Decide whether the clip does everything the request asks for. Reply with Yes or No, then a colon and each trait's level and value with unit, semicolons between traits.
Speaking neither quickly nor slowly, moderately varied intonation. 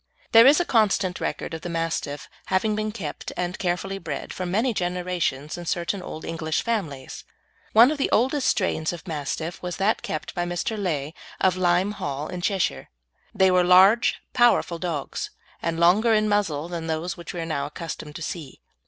Yes: average, 180 wpm; average, 3.8 semitones